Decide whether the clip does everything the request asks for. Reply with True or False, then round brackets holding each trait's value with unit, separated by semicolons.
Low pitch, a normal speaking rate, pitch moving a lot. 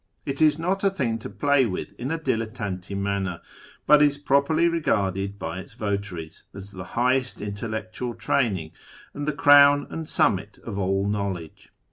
True (110 Hz; 165 wpm; 6.4 semitones)